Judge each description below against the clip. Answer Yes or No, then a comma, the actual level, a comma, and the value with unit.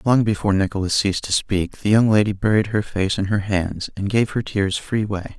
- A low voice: Yes, low, 100 Hz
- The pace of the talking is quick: Yes, fast, 235 wpm